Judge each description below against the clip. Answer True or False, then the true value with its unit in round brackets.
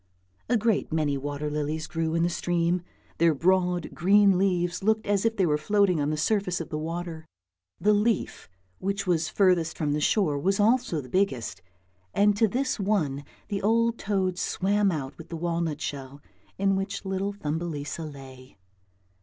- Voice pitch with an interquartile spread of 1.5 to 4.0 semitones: False (4.5 semitones)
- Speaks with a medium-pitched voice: True (175 Hz)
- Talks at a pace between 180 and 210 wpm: False (170 wpm)